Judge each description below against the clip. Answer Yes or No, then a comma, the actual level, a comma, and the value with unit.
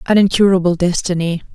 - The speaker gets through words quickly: No, slow, 115 wpm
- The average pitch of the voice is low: No, medium, 180 Hz